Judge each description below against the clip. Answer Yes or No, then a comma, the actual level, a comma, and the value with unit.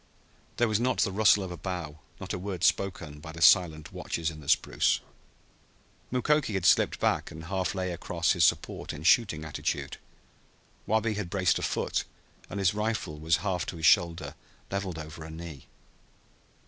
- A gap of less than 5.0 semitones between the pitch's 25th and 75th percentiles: Yes, average, 3.8 semitones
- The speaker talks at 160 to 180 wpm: Yes, average, 175 wpm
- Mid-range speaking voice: No, very low, 90 Hz